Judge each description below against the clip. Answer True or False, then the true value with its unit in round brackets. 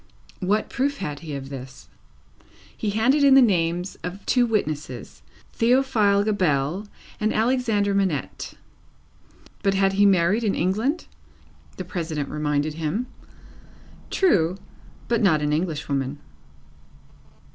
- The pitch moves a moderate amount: False (6.2 semitones)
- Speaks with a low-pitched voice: False (190 Hz)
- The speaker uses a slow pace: True (120 wpm)